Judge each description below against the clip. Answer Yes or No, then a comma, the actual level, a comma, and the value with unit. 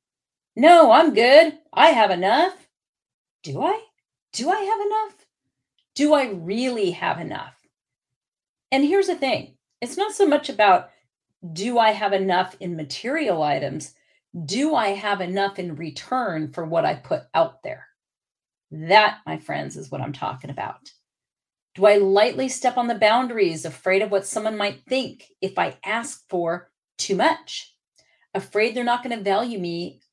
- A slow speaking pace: No, average, 155 wpm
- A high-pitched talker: Yes, high, 220 Hz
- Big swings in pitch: Yes, wide, 7.4 semitones